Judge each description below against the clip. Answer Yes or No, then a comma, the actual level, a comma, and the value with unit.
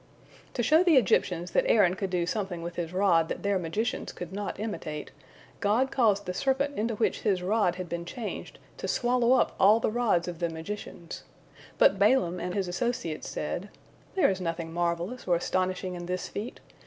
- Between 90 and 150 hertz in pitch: No, high, 190 Hz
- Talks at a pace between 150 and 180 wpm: No, average, 190 wpm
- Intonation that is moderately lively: Yes, average, 4.3 semitones